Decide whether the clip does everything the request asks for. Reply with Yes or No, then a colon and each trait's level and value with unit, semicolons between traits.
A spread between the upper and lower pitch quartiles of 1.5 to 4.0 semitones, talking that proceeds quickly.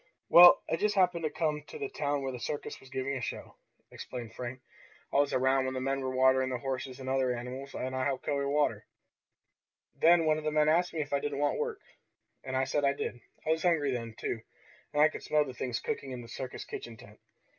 Yes: average, 2.9 semitones; fast, 240 wpm